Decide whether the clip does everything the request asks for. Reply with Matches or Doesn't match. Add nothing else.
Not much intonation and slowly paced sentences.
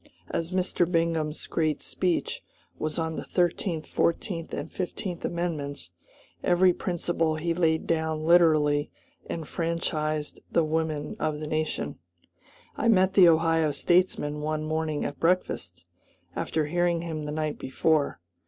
Matches